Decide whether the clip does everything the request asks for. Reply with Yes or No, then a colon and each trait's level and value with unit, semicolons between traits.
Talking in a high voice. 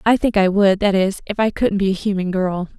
Yes: high, 195 Hz